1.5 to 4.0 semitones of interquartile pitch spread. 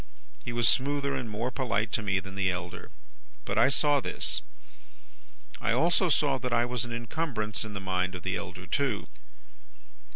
No: wide, 5.4 semitones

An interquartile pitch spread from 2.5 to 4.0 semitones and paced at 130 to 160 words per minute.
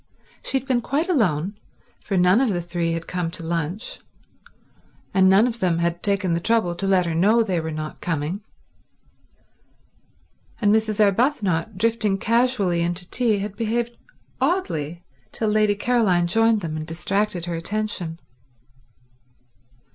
No: average, 4.7 semitones; average, 145 wpm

